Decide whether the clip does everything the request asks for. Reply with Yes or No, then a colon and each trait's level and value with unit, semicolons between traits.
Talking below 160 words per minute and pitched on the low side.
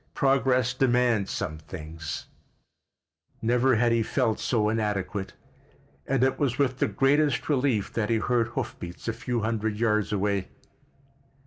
Yes: average, 140 wpm; low, 115 Hz